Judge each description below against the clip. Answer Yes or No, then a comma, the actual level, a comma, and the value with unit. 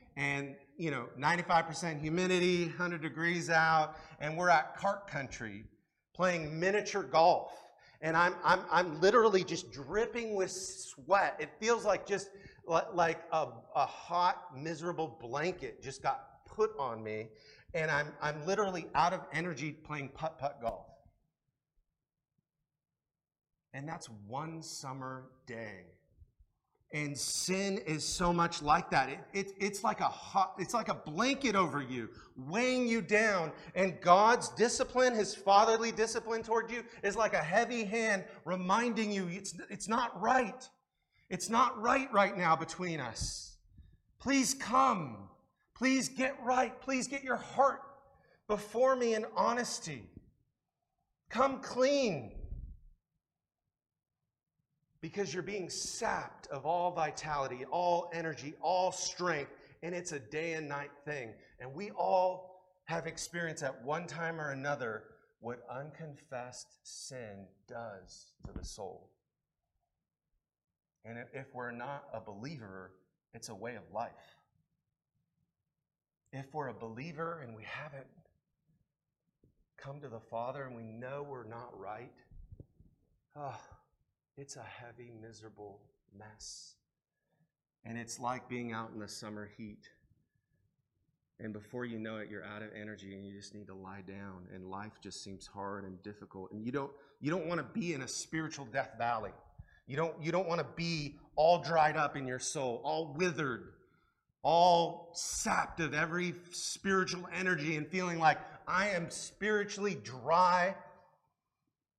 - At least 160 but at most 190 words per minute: No, average, 140 wpm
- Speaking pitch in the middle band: Yes, medium, 160 Hz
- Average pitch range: No, wide, 6.6 semitones